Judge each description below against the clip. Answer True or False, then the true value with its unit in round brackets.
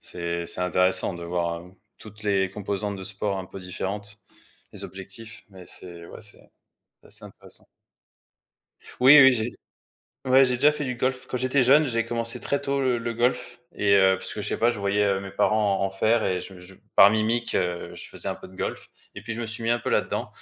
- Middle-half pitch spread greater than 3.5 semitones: True (3.9 semitones)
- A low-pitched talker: True (105 Hz)